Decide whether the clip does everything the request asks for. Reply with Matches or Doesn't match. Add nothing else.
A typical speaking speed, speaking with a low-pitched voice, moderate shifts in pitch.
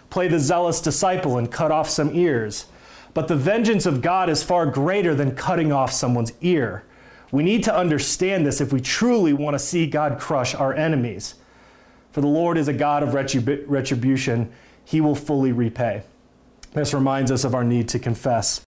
Doesn't match